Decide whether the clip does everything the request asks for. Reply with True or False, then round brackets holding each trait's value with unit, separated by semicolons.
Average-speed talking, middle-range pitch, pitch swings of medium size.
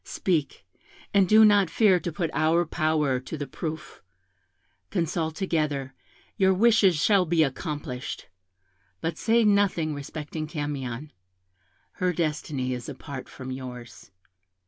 False (125 wpm; 155 Hz; 4.4 semitones)